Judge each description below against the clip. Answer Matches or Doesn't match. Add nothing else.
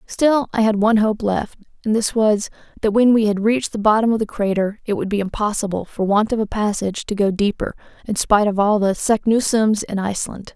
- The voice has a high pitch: Matches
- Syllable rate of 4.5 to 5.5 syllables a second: Doesn't match